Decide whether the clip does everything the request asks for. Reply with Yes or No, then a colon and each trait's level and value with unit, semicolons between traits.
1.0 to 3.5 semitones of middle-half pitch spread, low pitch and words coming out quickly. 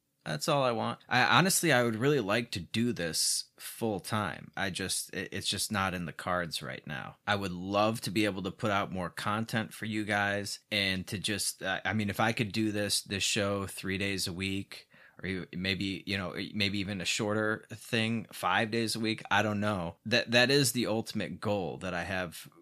Yes: narrow, 2.5 semitones; low, 105 Hz; fast, 220 wpm